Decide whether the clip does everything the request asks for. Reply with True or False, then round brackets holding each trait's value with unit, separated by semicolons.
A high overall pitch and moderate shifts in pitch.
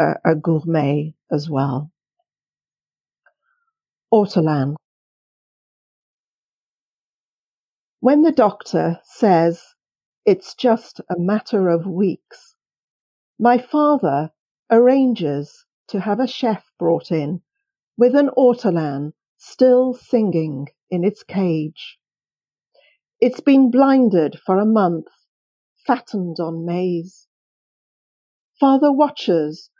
False (200 Hz; 7.9 semitones)